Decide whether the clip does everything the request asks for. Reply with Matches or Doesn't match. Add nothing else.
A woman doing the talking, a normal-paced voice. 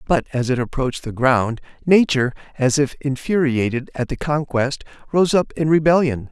Doesn't match